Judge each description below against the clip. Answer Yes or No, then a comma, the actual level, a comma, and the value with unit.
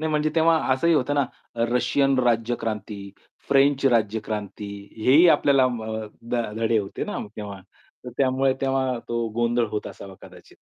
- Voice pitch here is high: No, low, 125 Hz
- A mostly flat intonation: No, average, 3.8 semitones